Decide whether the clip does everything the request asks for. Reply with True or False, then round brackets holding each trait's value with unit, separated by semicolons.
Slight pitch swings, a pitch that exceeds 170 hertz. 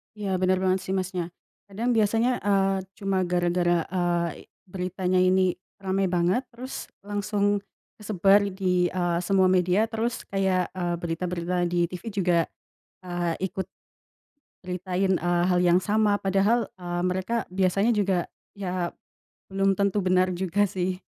True (1.7 semitones; 185 Hz)